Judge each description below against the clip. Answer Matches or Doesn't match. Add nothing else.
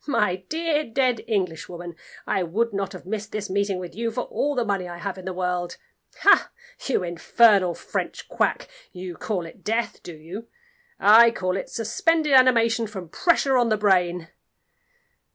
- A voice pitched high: Matches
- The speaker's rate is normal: Matches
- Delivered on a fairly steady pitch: Doesn't match